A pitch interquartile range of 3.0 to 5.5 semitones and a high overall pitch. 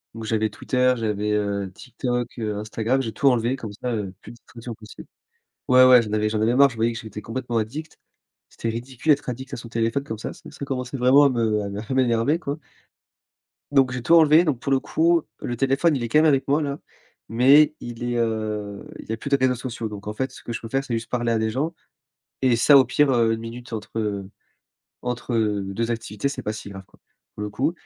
No: average, 3.3 semitones; low, 120 Hz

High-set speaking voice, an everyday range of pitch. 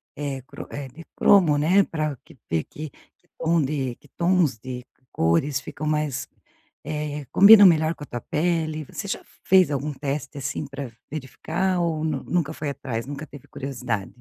No: medium, 150 Hz; average, 3.1 semitones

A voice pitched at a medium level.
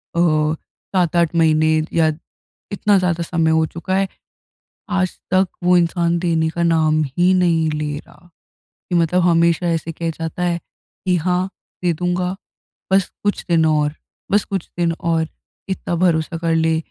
Yes: medium, 170 Hz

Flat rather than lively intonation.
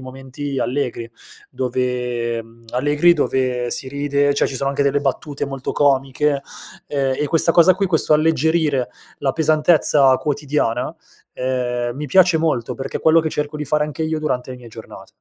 No: average, 3.0 semitones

